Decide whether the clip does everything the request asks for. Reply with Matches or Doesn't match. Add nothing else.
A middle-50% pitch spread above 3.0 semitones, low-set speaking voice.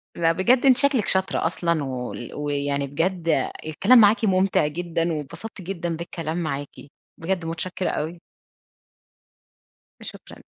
Doesn't match